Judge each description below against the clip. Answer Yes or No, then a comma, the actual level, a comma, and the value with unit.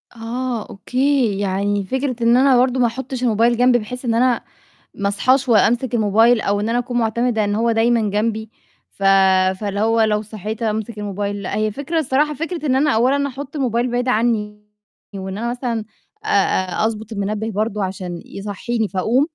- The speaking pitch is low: No, high, 225 Hz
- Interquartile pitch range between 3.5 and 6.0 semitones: No, average, 3.1 semitones